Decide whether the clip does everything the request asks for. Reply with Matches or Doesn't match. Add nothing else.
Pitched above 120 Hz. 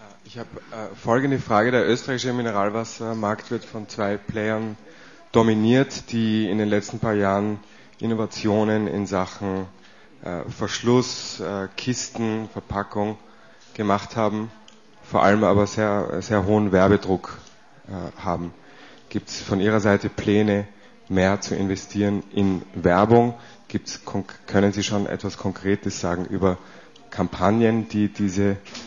Doesn't match